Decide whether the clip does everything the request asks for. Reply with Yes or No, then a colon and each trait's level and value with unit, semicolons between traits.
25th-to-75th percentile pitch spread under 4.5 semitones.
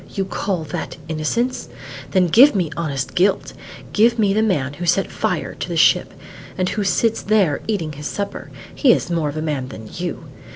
No: average, 5.3 semitones